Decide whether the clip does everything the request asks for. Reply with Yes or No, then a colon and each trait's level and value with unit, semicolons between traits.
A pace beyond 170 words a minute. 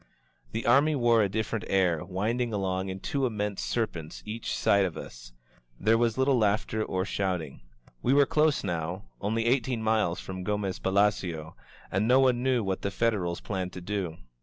Yes: average, 180 wpm